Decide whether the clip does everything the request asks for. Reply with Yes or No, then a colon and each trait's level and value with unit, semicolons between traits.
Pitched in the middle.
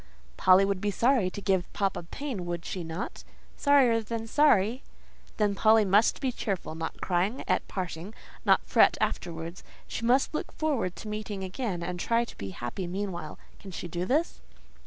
No: high, 195 Hz